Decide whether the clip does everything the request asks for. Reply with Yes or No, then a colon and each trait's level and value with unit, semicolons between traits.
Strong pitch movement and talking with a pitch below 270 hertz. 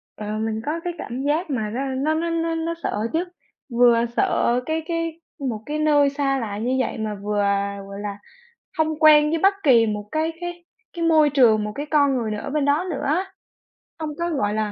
No: wide, 6.3 semitones; very high, 285 Hz